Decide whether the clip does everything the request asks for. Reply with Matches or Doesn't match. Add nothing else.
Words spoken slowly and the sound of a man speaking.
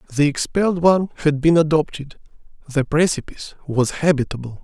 Matches